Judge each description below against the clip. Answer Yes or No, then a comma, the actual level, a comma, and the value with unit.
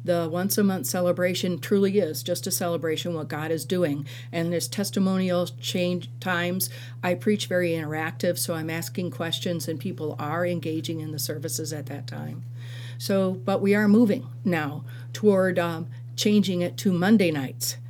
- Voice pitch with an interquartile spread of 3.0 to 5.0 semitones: Yes, average, 4.7 semitones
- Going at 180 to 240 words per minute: No, average, 170 wpm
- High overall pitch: No, medium, 165 Hz